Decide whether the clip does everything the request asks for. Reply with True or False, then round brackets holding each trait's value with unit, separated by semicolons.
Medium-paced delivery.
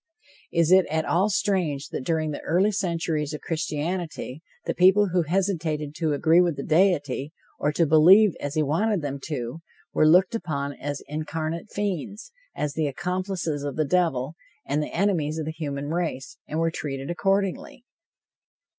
True (165 wpm)